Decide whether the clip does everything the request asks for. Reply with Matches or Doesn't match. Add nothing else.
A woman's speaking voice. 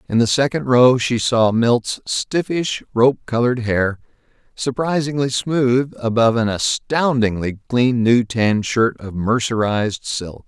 Doesn't match